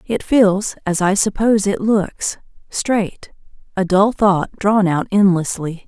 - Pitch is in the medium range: No, high, 195 Hz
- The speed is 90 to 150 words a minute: Yes, slow, 135 wpm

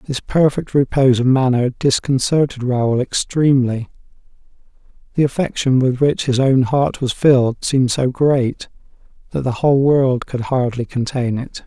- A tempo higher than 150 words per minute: No, average, 145 wpm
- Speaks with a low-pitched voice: Yes, low, 130 Hz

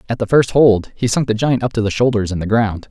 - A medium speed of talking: No, fast, 310 wpm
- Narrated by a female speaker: No, male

